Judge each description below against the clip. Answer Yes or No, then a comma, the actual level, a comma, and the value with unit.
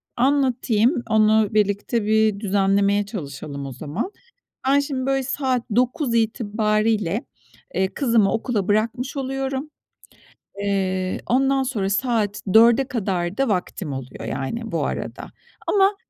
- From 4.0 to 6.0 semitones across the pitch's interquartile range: Yes, average, 4.6 semitones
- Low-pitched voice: No, high, 220 Hz